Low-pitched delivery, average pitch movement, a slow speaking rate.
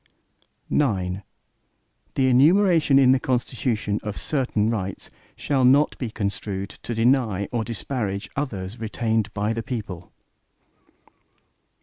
Yes: low, 115 Hz; average, 4.4 semitones; slow, 110 wpm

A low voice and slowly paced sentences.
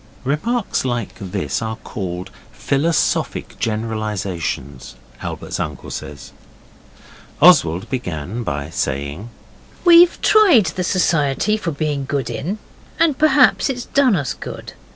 Yes: low, 130 Hz; slow, 110 wpm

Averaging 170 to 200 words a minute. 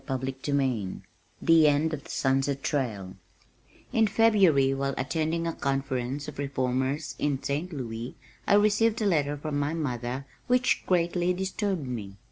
No: average, 145 wpm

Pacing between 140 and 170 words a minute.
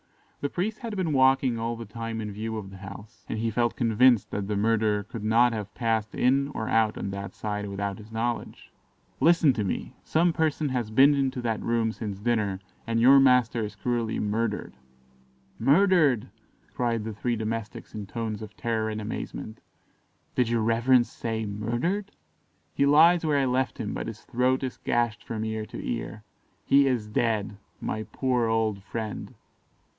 No: average, 180 wpm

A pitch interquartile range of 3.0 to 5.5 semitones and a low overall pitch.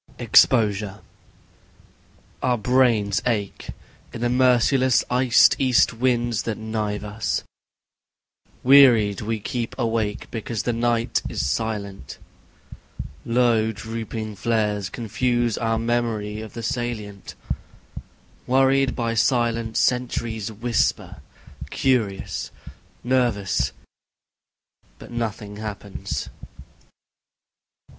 No: narrow, 2.4 semitones; low, 115 Hz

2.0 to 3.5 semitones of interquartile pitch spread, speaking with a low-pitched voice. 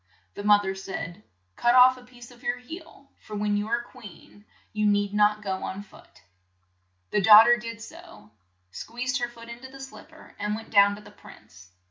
No: average, 3.2 semitones; high, 215 Hz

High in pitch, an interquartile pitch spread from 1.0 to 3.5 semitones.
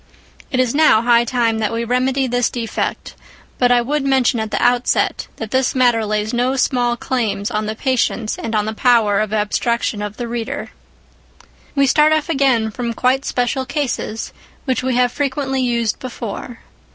Yes: high, 245 Hz; average, 2.7 semitones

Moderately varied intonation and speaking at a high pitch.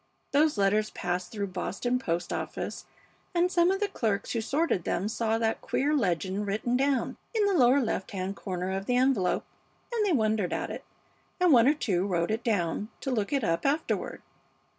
No: wide, 6.2 semitones; high, 220 Hz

